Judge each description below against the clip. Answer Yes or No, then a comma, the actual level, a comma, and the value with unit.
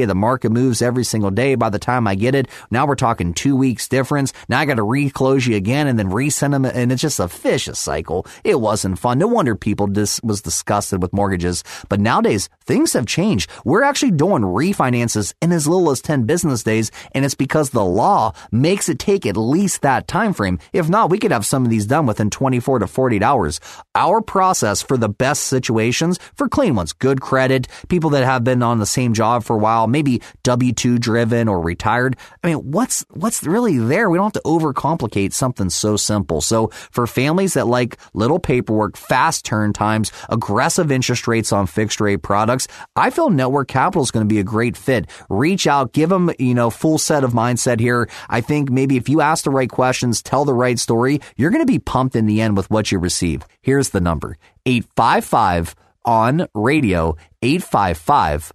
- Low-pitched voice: Yes, low, 125 Hz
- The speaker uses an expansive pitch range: No, average, 4.6 semitones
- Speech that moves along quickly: Yes, fast, 210 wpm